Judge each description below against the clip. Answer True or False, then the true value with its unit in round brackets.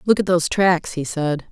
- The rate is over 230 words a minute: True (240 wpm)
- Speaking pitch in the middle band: True (170 Hz)